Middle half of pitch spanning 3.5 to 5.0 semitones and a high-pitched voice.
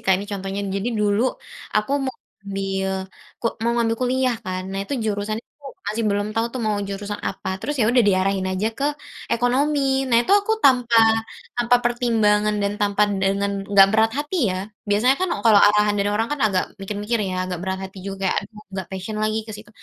No: average, 3.1 semitones; high, 210 Hz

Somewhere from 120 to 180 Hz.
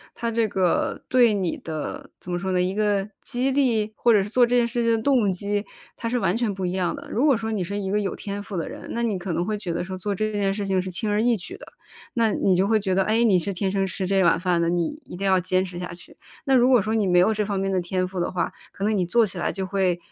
No: high, 200 Hz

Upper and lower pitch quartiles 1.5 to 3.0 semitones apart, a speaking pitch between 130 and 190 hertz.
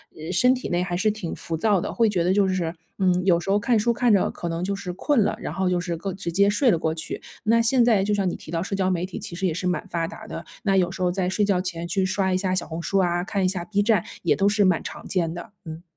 Yes: average, 2.7 semitones; medium, 185 Hz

